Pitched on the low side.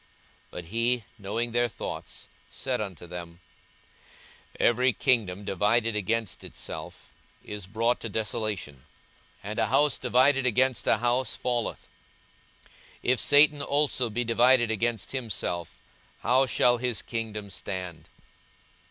Yes: low, 115 Hz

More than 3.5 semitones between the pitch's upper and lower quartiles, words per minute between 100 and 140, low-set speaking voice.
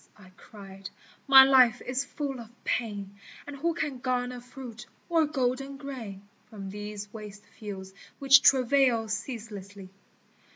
No: average, 4.7 semitones; slow, 135 wpm; high, 240 Hz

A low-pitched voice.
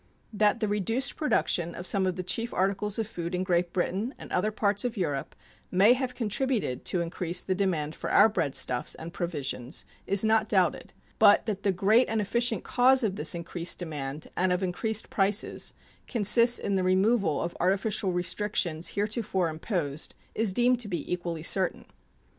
No: high, 190 Hz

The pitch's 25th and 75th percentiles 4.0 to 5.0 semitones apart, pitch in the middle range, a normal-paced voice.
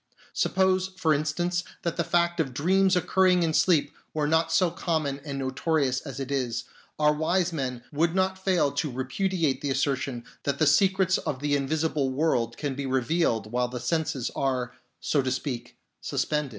Yes: average, 4.3 semitones; medium, 150 Hz; average, 175 wpm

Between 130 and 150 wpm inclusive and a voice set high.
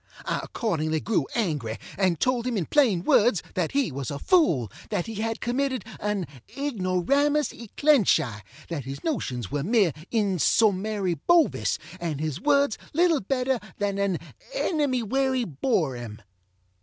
Yes: average, 140 wpm; high, 205 Hz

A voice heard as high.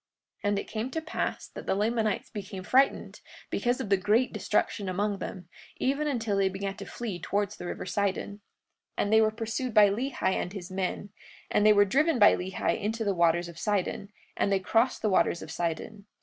Yes: high, 205 Hz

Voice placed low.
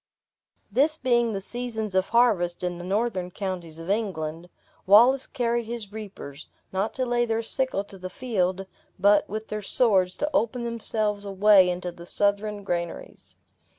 No: high, 205 Hz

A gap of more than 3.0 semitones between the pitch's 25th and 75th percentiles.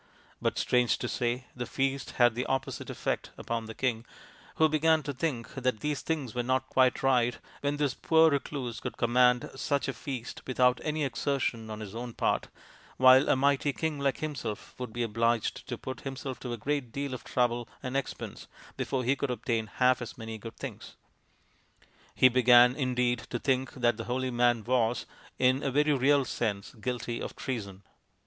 No: narrow, 2.5 semitones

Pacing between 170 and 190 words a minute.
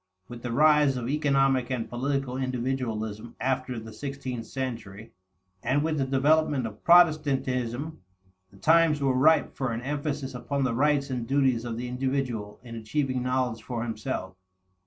No: average, 155 wpm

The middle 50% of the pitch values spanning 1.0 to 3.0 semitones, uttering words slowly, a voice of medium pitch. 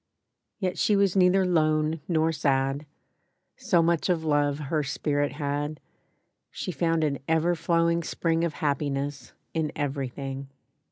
Yes: average, 2.7 semitones; slow, 130 wpm; medium, 155 Hz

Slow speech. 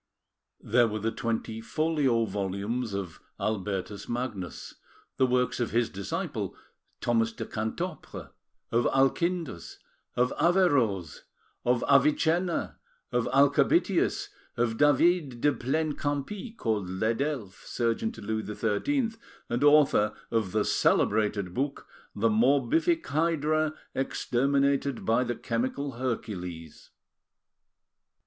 Yes: slow, 105 wpm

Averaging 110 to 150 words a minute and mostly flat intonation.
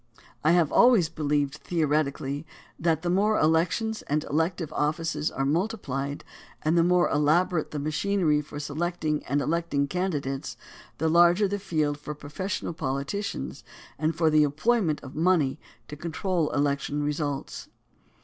No: average, 145 wpm; average, 3.1 semitones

